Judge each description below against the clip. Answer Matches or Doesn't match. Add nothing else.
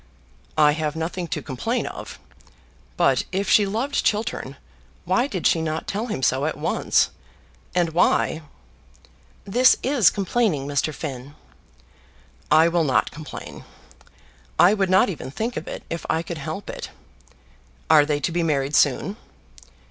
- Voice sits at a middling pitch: Matches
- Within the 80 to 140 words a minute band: Doesn't match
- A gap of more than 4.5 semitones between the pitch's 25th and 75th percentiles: Matches